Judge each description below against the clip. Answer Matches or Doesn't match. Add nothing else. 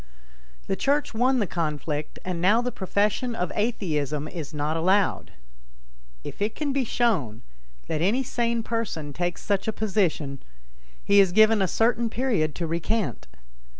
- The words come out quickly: Doesn't match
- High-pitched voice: Matches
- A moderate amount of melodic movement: Doesn't match